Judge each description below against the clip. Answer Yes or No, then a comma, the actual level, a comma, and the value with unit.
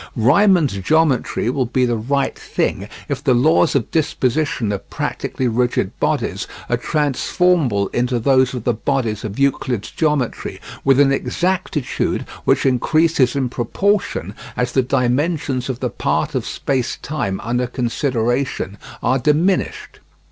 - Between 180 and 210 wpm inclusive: No, slow, 135 wpm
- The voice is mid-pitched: No, low, 130 Hz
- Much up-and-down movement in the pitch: No, average, 3.5 semitones